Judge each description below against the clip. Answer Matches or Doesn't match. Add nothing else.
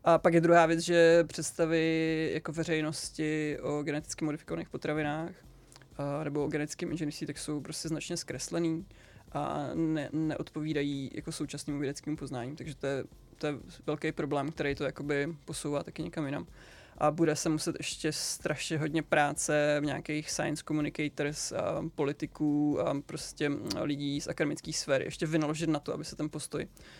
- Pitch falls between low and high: Matches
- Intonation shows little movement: Matches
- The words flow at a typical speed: Matches